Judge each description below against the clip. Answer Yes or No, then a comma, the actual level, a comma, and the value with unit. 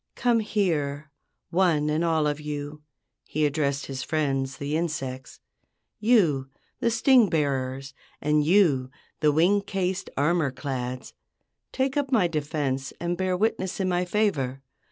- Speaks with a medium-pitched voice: Yes, medium, 155 Hz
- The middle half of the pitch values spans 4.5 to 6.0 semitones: Yes, average, 5.1 semitones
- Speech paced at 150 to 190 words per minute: No, slow, 135 wpm